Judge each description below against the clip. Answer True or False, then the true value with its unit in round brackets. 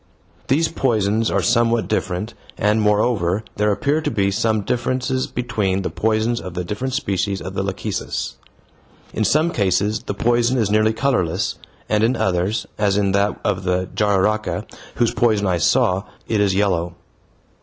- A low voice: True (105 Hz)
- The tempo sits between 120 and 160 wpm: True (155 wpm)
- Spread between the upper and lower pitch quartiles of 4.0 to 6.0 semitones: False (3.3 semitones)